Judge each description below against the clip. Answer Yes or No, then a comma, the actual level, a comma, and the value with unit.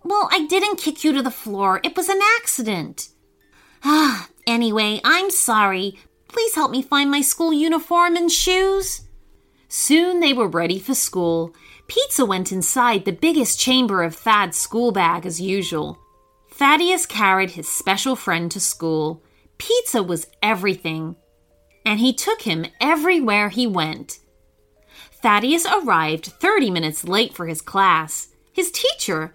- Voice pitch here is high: Yes, high, 225 Hz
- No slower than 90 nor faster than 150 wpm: Yes, average, 145 wpm